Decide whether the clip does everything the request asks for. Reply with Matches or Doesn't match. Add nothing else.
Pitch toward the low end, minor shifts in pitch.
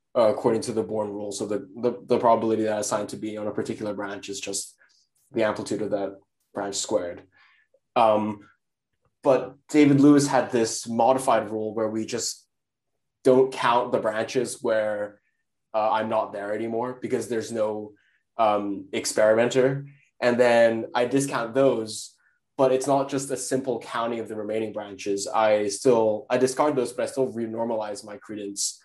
Doesn't match